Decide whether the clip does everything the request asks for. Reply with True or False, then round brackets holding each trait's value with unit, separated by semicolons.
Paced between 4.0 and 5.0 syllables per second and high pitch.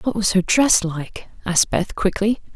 True (4.5 syllables/s; 200 Hz)